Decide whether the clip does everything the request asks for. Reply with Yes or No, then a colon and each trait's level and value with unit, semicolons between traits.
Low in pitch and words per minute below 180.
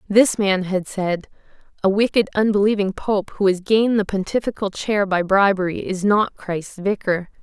No: high, 200 Hz; average, 160 wpm